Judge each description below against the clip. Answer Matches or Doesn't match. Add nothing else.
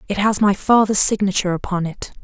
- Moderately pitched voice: Doesn't match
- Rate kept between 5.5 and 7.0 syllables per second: Matches